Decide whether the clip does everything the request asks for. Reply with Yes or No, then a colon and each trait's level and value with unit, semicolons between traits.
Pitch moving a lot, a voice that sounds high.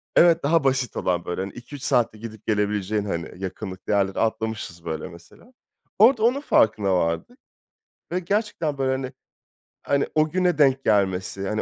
No: wide, 7.7 semitones; low, 110 Hz